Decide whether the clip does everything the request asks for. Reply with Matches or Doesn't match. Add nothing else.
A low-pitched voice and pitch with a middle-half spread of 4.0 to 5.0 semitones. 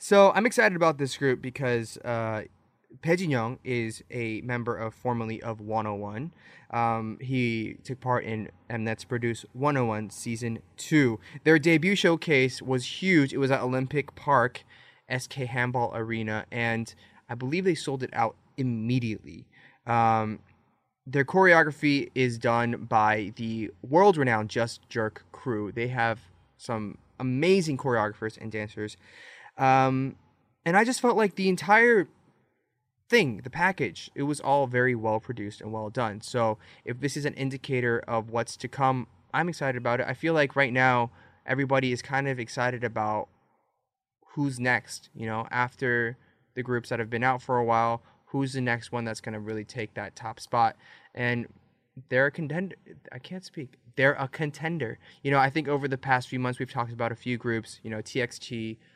Doesn't match